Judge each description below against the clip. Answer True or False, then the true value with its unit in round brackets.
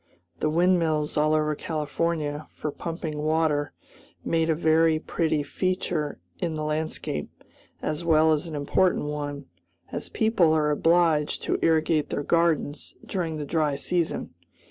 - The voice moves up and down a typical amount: False (1.8 semitones)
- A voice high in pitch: False (155 Hz)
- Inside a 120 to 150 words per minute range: True (140 wpm)